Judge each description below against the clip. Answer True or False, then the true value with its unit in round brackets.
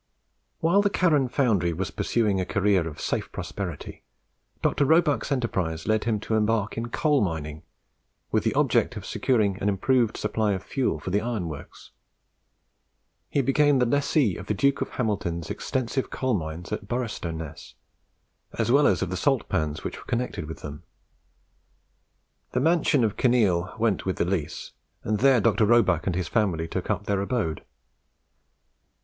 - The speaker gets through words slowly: False (165 wpm)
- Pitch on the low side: True (105 Hz)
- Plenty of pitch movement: True (6.0 semitones)